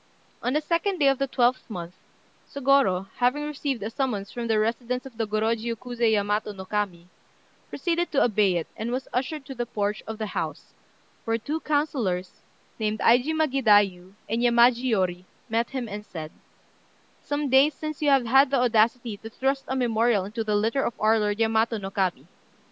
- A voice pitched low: No, high, 230 Hz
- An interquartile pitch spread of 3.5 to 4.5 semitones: Yes, average, 4.2 semitones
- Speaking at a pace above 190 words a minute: No, average, 180 wpm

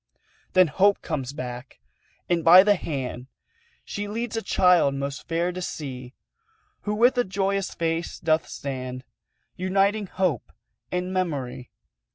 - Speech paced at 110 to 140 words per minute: Yes, slow, 135 wpm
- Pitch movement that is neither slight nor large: No, wide, 5.9 semitones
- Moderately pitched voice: Yes, medium, 175 Hz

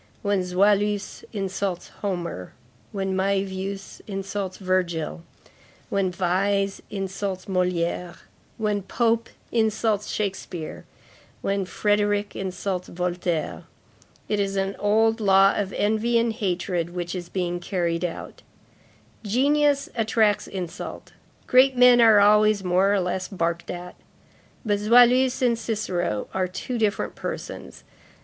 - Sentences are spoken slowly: Yes, slow, 115 wpm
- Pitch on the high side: Yes, high, 195 Hz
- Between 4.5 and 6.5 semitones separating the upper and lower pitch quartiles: No, average, 2.7 semitones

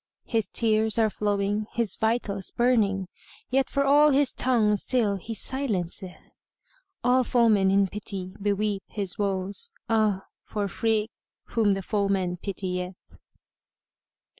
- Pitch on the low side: No, high, 210 Hz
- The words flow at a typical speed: No, slow, 130 wpm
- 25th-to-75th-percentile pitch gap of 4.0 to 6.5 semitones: No, average, 2.9 semitones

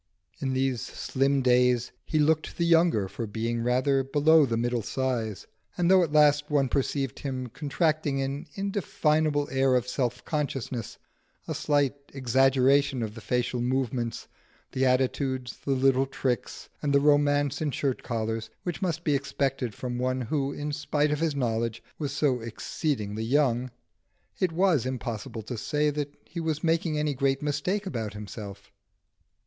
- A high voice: No, low, 135 Hz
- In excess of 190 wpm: No, average, 155 wpm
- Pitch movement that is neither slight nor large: Yes, average, 3.3 semitones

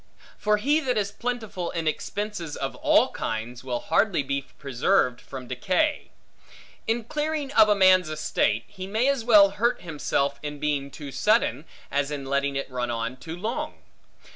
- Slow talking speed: No, average, 165 wpm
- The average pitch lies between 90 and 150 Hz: No, medium, 170 Hz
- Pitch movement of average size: No, wide, 7.7 semitones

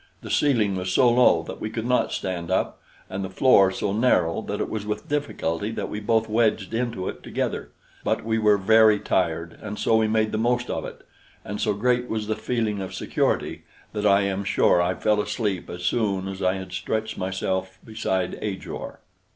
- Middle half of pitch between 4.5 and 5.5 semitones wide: No, average, 2.9 semitones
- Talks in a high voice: No, low, 105 Hz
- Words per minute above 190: Yes, average, 200 wpm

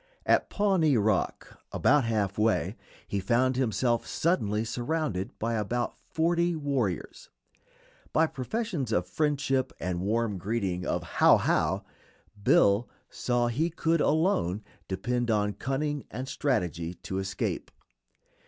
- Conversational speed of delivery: No, slow, 120 wpm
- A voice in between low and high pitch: No, low, 120 Hz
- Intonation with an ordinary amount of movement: No, wide, 6.4 semitones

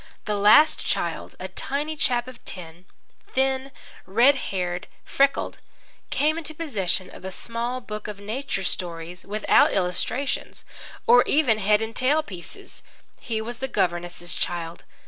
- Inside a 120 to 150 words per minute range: Yes, average, 140 wpm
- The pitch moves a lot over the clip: Yes, wide, 6.2 semitones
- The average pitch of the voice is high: Yes, high, 220 Hz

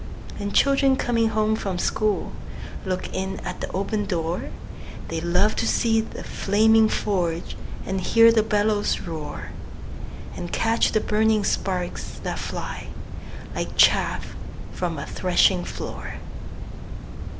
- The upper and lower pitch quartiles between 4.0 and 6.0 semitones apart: No, average, 3.1 semitones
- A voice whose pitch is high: Yes, high, 205 Hz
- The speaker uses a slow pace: Yes, slow, 130 wpm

